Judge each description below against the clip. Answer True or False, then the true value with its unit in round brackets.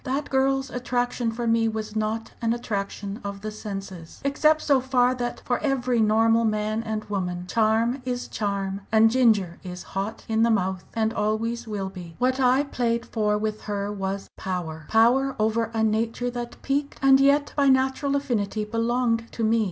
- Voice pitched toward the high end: True (225 Hz)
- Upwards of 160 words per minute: True (175 wpm)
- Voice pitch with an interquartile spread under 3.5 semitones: True (3.0 semitones)